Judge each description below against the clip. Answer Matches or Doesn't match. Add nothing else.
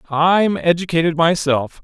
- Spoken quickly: Doesn't match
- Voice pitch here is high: Doesn't match